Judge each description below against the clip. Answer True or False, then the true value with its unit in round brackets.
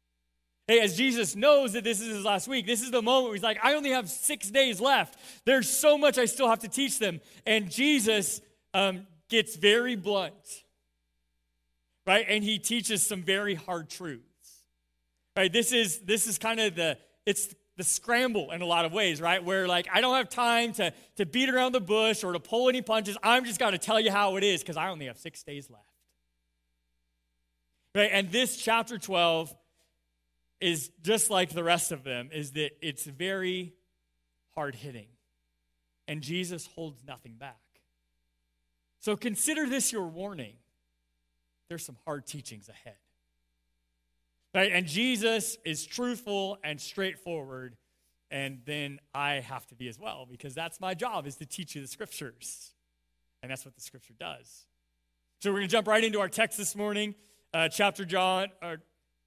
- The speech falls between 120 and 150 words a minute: False (175 wpm)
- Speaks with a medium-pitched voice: True (175 Hz)